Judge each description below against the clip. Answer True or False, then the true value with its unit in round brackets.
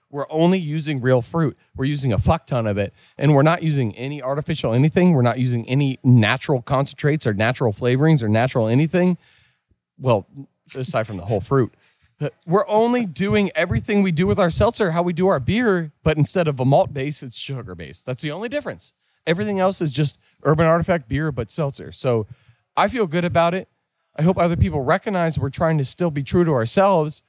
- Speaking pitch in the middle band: True (145 Hz)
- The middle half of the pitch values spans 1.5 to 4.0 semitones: False (5.3 semitones)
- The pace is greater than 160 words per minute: True (205 wpm)